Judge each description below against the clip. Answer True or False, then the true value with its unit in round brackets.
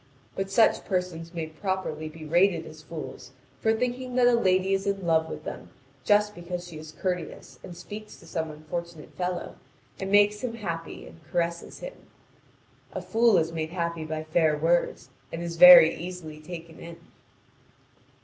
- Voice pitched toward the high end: False (170 Hz)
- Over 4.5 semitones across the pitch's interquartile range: False (3.4 semitones)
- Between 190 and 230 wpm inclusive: False (170 wpm)